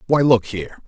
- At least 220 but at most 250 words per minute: No, fast, 205 wpm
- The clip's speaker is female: No, male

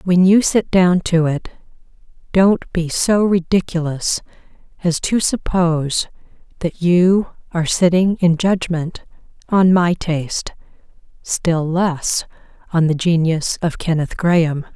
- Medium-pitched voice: Yes, medium, 170 Hz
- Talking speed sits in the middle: No, slow, 120 wpm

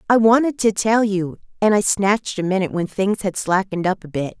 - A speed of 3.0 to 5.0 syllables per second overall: No, 5.8 syllables/s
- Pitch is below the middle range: No, high, 200 Hz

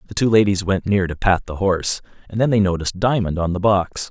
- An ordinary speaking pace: No, fast, 250 wpm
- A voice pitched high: No, very low, 95 Hz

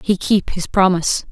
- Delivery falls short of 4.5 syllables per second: No, 5.0 syllables/s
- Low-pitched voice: No, medium, 185 Hz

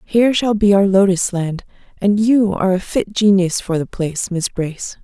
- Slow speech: No, average, 200 wpm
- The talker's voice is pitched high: Yes, high, 195 Hz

